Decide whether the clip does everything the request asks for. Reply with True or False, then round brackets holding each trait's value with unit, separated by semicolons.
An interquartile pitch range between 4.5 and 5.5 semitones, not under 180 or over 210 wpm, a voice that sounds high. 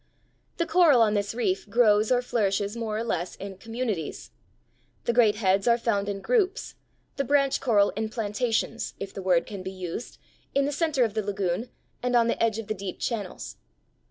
False (3.5 semitones; 190 wpm; 220 Hz)